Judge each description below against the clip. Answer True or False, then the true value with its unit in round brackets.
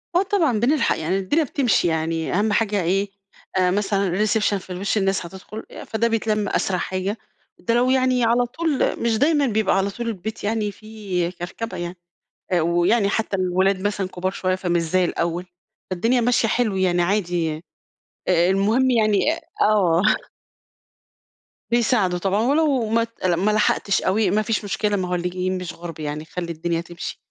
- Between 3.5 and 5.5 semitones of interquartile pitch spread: True (4.0 semitones)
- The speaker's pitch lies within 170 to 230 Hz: True (200 Hz)